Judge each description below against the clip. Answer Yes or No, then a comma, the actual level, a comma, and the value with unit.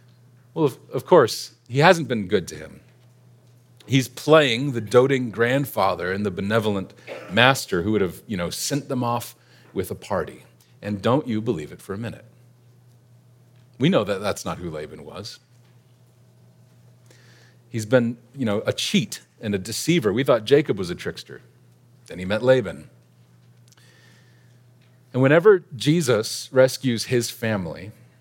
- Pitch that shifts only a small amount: Yes, narrow, 1.3 semitones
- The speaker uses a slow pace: No, average, 150 wpm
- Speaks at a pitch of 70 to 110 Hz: No, low, 125 Hz